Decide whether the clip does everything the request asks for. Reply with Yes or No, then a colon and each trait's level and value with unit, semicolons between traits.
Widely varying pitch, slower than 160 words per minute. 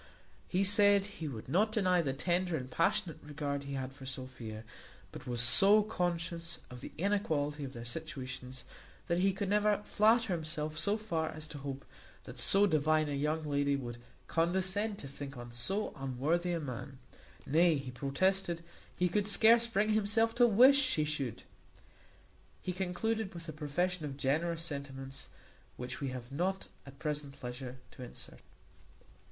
No: wide, 6.0 semitones; average, 165 wpm